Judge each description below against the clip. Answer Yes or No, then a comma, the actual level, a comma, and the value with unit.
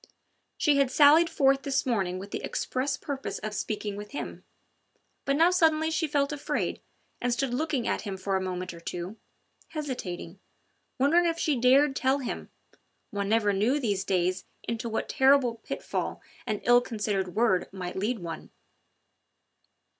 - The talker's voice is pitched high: Yes, high, 240 Hz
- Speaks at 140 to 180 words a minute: Yes, average, 160 wpm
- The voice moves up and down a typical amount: No, wide, 6.1 semitones